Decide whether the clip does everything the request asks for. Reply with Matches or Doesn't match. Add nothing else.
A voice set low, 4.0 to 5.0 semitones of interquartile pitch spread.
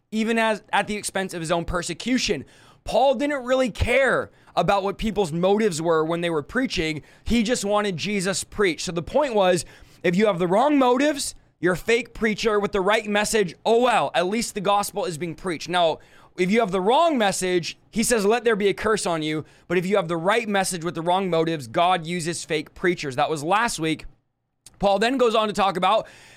Doesn't match